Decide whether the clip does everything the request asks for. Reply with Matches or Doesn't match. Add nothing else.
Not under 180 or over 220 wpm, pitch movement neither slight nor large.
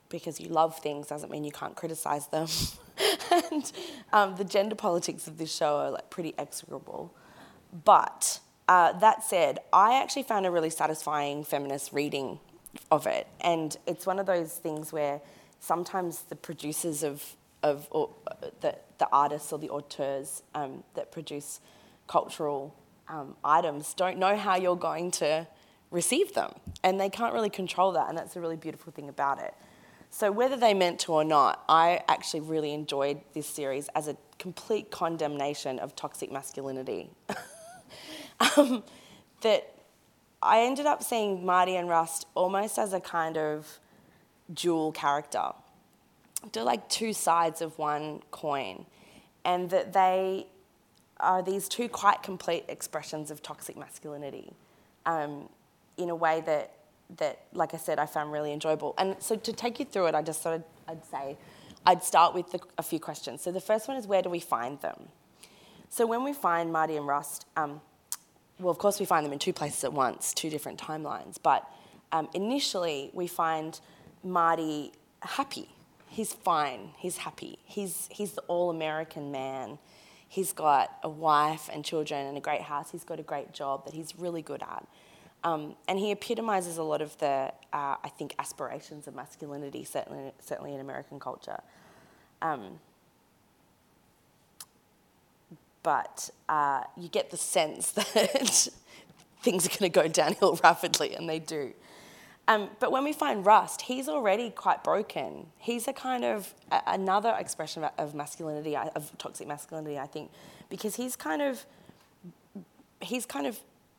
Doesn't match